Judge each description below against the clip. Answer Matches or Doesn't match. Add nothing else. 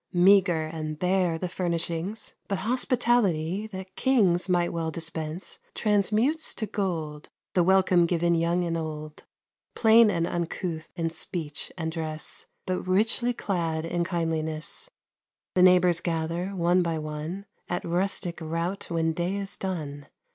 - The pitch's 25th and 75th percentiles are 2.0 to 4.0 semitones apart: Matches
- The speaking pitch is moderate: Matches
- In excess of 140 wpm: Doesn't match